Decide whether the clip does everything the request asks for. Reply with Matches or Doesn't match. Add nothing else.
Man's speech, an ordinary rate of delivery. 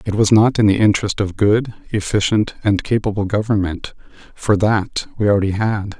Matches